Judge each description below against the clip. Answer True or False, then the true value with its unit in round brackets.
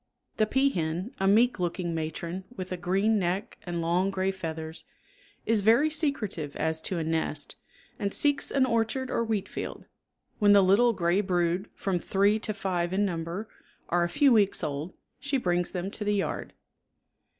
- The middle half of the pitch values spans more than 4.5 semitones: False (3.9 semitones)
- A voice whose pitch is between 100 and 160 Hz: False (190 Hz)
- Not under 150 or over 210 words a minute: True (170 wpm)